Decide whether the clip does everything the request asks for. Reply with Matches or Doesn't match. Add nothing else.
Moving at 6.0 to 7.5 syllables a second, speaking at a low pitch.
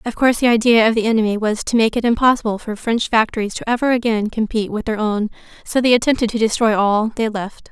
Doesn't match